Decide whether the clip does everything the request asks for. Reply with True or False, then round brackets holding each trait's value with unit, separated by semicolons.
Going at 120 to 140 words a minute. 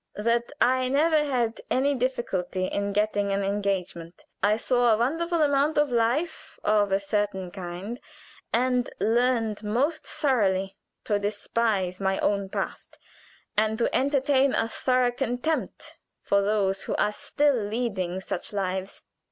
True (135 wpm)